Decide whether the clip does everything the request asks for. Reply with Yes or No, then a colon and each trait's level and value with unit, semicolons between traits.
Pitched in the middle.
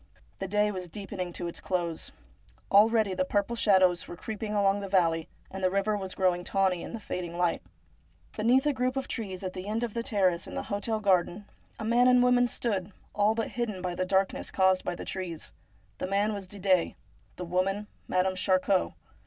No: high, 195 Hz